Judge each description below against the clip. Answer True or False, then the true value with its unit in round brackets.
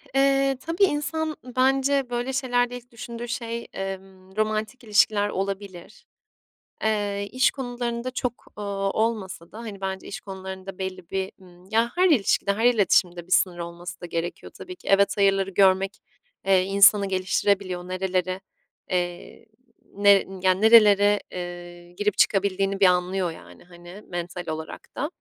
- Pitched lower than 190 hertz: False (195 Hz)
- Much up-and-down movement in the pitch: False (4.2 semitones)